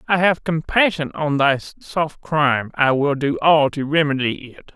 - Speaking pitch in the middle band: Yes, medium, 150 Hz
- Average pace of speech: Yes, average, 165 wpm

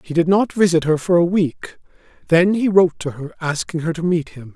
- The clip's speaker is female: No, male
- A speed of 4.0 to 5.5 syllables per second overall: No, 5.8 syllables/s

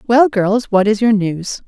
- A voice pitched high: Yes, high, 210 Hz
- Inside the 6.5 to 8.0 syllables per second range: No, 4.0 syllables/s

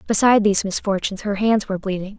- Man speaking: No, female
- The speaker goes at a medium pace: Yes, average, 190 wpm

